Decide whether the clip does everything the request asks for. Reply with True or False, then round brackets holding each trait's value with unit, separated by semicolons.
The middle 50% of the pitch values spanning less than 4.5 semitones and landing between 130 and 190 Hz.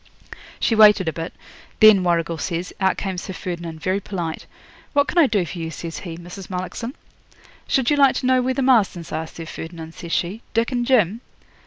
False (5.4 semitones; 185 Hz)